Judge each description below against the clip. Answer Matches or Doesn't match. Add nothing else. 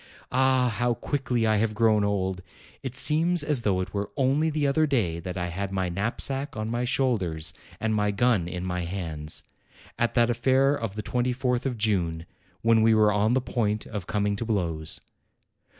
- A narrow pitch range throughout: Doesn't match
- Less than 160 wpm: Doesn't match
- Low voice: Matches